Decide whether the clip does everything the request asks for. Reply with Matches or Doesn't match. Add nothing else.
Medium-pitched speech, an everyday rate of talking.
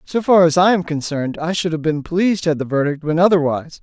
Doesn't match